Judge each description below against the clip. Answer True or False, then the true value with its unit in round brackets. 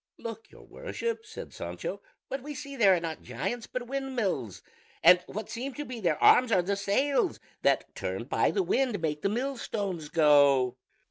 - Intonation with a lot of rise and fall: True (8.0 semitones)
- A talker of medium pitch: False (220 Hz)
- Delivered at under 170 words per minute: False (180 wpm)